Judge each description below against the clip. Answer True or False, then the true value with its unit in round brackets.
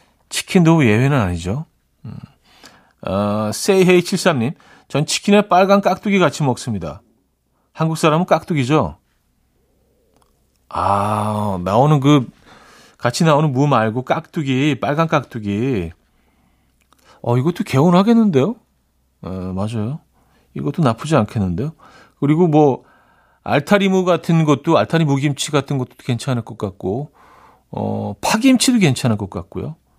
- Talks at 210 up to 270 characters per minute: True (260 characters per minute)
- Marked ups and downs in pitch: True (7.7 semitones)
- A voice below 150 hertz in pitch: True (140 Hz)